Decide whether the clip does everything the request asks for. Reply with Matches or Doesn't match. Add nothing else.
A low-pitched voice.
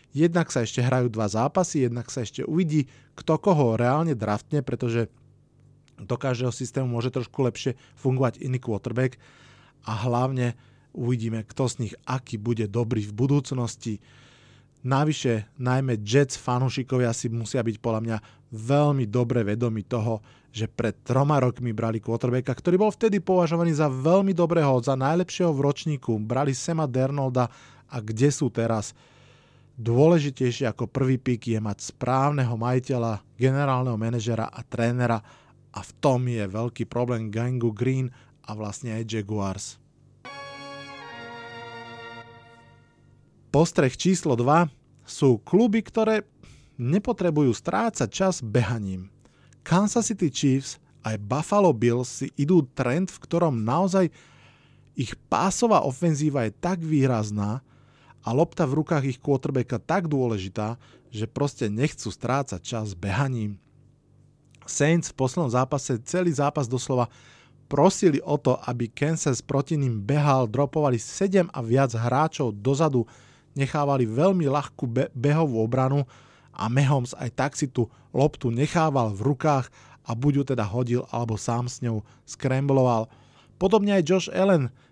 Matches